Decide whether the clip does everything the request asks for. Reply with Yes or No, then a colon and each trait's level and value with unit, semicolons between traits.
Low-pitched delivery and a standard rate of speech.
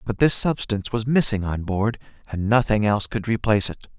Yes: low, 110 Hz; average, 195 wpm